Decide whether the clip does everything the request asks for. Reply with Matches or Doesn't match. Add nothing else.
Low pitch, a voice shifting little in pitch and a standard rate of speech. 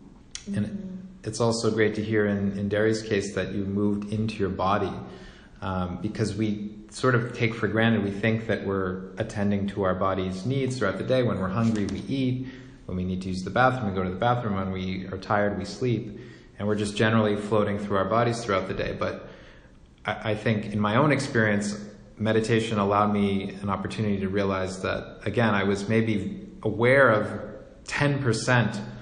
Matches